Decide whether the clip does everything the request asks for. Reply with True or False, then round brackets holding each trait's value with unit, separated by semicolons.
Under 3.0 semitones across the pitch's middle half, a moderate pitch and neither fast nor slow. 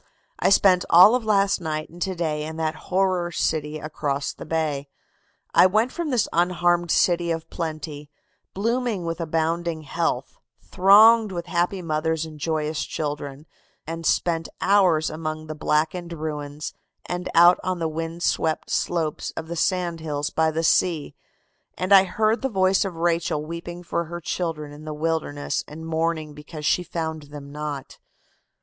True (2.5 semitones; 165 Hz; 160 wpm)